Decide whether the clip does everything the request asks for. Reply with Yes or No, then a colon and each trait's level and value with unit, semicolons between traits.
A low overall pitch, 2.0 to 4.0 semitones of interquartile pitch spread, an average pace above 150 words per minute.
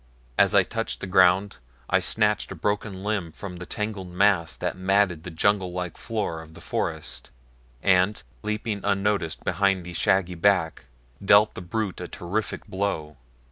Yes: very low, 95 Hz; narrow, 2.6 semitones; average, 160 wpm